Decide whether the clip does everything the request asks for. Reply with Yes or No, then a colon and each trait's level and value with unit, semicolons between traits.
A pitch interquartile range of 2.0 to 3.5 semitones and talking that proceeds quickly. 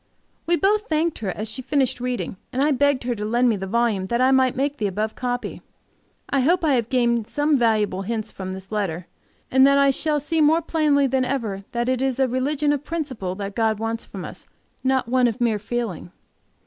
No: average, 4.3 semitones; fast, 220 wpm